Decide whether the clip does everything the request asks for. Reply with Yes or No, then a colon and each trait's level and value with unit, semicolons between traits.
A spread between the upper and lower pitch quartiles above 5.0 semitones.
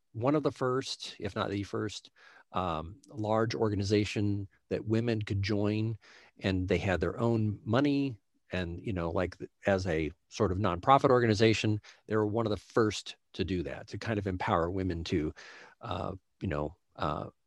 No: average, 3.2 semitones